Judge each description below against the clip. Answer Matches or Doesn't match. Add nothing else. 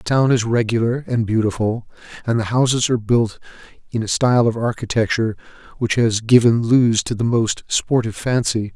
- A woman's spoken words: Doesn't match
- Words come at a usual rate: Matches